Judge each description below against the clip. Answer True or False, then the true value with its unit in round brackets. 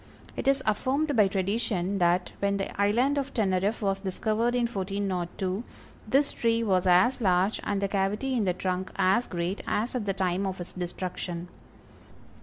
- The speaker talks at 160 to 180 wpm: True (170 wpm)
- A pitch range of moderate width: True (3.7 semitones)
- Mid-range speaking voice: False (195 Hz)